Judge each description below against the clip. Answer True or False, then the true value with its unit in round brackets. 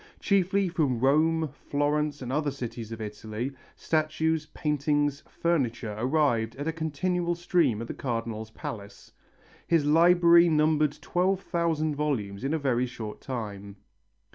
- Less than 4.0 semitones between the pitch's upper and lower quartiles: False (5.4 semitones)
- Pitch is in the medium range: True (145 Hz)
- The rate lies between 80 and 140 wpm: True (135 wpm)